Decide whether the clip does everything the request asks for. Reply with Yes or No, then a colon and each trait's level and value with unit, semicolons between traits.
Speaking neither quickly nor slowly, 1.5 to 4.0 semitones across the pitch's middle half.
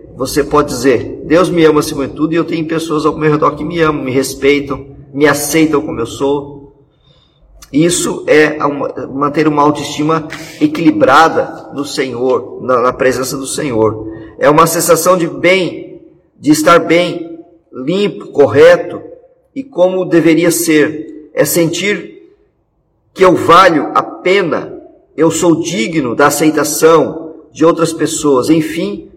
Yes: average, 140 wpm; average, 2.8 semitones